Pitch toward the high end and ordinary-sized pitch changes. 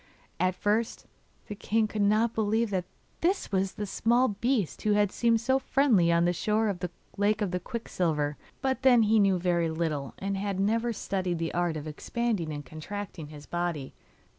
Yes: high, 200 Hz; average, 4.5 semitones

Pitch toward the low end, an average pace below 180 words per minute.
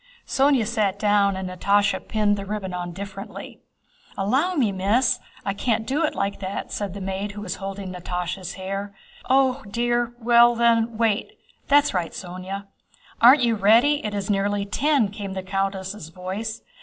No: high, 205 Hz; average, 165 wpm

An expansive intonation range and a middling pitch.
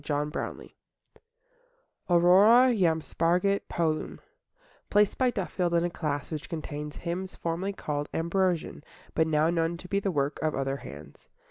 No: average, 3.5 semitones; medium, 170 Hz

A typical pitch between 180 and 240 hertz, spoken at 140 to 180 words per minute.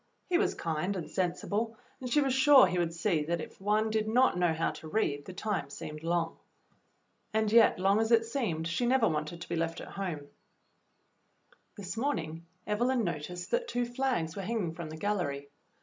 No: high, 190 Hz; average, 195 wpm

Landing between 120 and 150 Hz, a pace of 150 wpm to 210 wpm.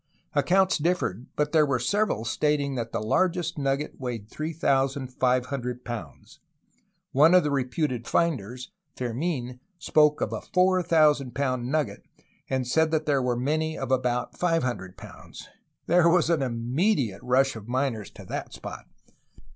No: low, 135 Hz; average, 140 wpm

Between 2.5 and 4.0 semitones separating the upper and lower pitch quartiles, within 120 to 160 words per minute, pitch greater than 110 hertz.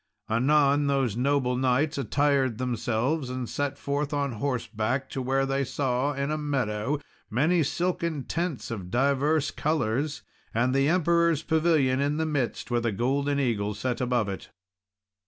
Yes: average, 3.0 semitones; average, 150 wpm; low, 135 Hz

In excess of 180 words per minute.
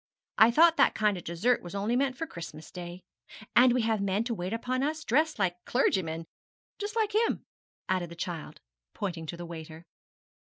Yes: average, 190 wpm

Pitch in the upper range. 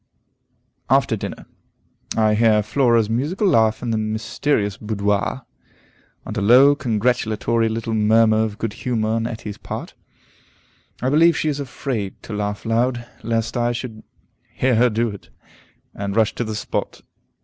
No: low, 115 Hz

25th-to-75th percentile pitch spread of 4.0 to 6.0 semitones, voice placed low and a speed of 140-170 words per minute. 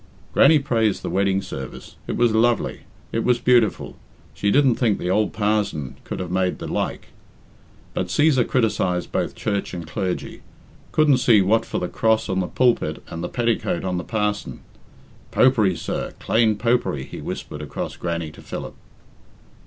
Yes: average, 4.7 semitones; low, 105 Hz; average, 165 wpm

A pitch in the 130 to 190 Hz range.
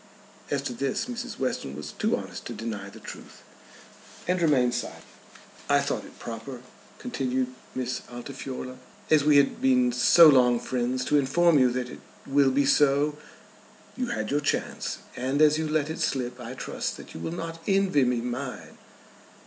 Yes: low, 135 Hz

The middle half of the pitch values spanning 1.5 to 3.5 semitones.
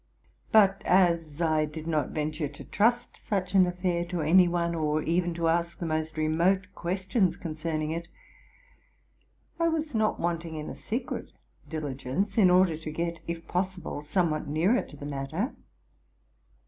Yes: average, 3.1 semitones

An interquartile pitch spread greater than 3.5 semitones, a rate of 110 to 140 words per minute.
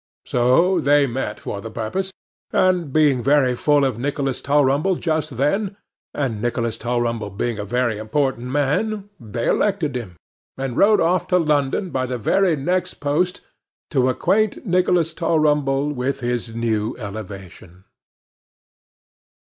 Yes: wide, 5.4 semitones; slow, 135 wpm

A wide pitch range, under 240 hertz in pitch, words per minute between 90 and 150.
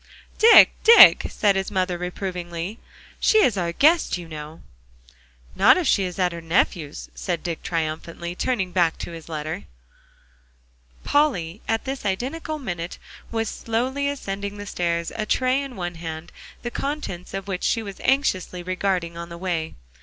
No: wide, 5.7 semitones; medium, 185 Hz; average, 160 wpm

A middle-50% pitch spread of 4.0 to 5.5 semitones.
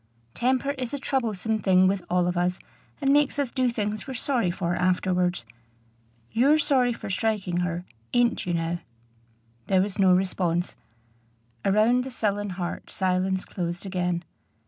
Yes: average, 5.2 semitones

